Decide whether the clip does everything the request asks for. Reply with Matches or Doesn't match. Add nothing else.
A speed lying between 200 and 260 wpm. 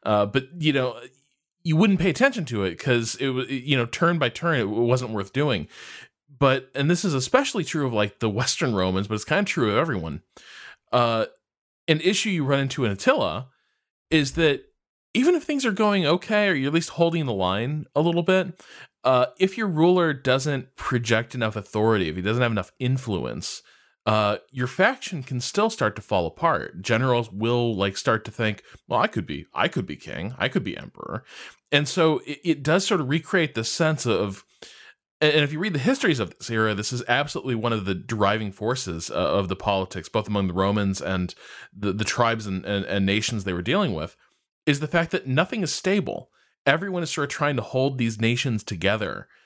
Matches